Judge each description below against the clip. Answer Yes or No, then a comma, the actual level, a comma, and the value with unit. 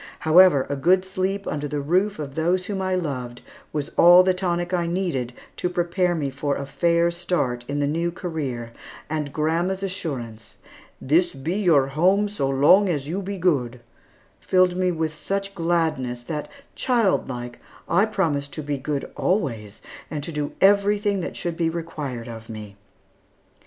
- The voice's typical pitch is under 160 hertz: No, medium, 165 Hz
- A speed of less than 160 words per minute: No, average, 165 wpm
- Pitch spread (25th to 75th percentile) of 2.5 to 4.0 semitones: No, average, 4.8 semitones